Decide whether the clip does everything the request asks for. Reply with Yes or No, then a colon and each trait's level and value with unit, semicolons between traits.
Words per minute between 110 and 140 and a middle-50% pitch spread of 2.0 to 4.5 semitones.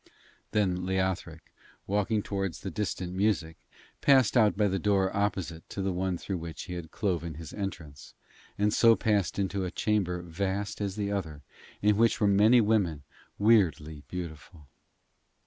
No: average, 155 wpm; average, 3.2 semitones